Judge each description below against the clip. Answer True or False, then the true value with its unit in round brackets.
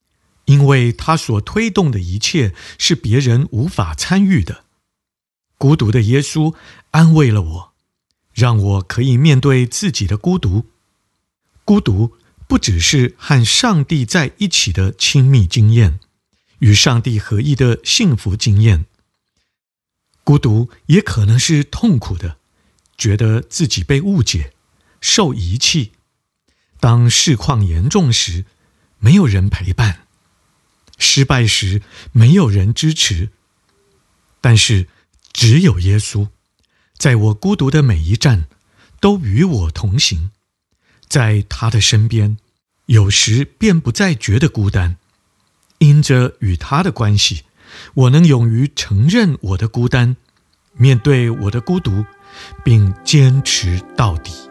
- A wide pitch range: True (5.7 semitones)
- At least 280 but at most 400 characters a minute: False (180 characters per minute)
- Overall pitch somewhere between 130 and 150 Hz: False (115 Hz)